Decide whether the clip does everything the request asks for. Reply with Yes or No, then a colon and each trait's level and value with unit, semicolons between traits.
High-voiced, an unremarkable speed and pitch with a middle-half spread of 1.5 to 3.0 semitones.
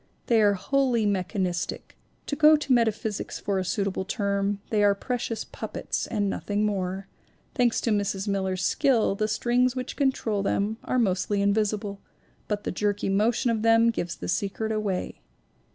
Yes: high, 210 Hz; average, 160 wpm; average, 2.7 semitones